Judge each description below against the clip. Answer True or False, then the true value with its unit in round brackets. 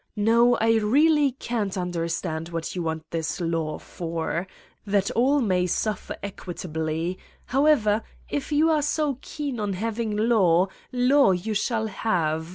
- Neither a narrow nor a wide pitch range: False (6.1 semitones)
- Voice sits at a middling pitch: False (210 Hz)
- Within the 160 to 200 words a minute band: False (145 wpm)